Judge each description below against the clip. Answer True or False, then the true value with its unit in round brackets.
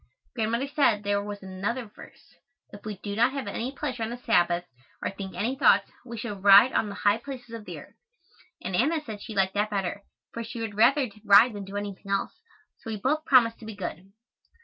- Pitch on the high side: True (215 Hz)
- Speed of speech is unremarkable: False (215 wpm)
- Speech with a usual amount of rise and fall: True (3.1 semitones)